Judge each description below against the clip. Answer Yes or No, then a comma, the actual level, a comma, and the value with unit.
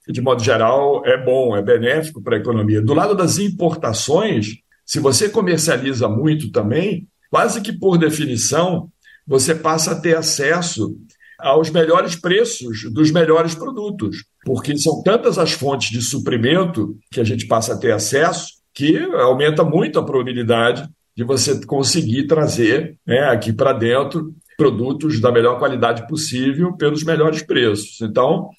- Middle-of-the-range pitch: Yes, medium, 155 Hz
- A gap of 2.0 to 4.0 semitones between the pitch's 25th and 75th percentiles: No, average, 4.8 semitones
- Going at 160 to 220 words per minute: No, average, 145 wpm